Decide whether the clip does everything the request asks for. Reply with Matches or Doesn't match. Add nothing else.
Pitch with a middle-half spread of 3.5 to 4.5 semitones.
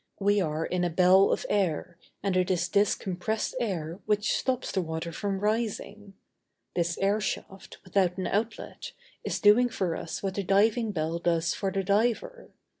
Doesn't match